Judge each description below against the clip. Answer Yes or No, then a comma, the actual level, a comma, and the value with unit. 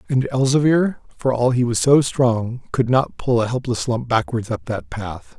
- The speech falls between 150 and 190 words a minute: No, average, 200 wpm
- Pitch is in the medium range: No, low, 120 Hz